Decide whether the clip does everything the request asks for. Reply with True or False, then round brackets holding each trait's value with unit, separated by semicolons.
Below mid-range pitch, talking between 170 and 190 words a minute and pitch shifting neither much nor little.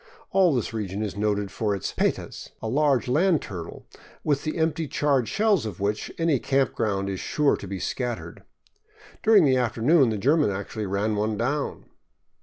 False (120 Hz; 175 wpm; 6.4 semitones)